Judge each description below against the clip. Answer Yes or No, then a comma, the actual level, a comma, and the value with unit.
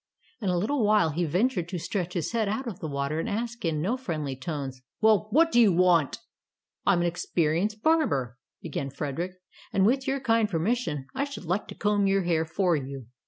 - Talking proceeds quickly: Yes, fast, 210 wpm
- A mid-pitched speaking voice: Yes, medium, 180 Hz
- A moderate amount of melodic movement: No, wide, 5.8 semitones